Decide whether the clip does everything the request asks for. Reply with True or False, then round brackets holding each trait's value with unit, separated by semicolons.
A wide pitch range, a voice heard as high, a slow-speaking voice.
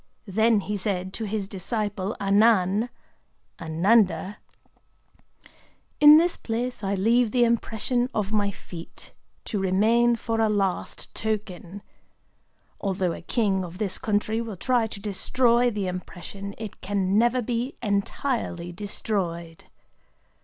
False (3.2 semitones; 210 Hz; 125 wpm)